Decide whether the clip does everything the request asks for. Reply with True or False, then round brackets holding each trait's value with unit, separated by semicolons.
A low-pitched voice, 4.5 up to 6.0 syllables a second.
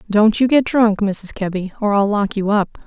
False (210 Hz; 4.8 syllables/s)